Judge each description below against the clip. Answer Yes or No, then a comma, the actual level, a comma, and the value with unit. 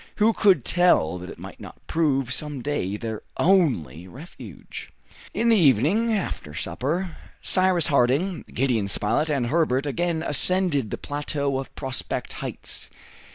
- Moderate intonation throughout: No, wide, 6.3 semitones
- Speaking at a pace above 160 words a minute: No, average, 140 wpm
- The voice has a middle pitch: Yes, medium, 145 Hz